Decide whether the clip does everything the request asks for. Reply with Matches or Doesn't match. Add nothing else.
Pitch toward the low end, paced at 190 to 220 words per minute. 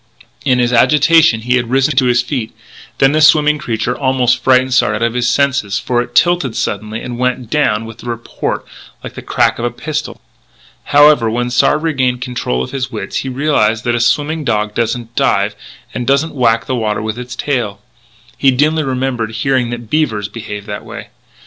Matches